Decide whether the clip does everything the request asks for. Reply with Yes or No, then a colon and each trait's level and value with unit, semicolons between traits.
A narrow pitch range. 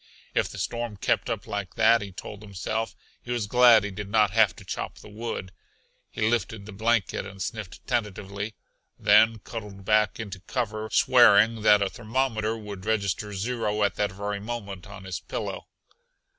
Yes: narrow, 2.1 semitones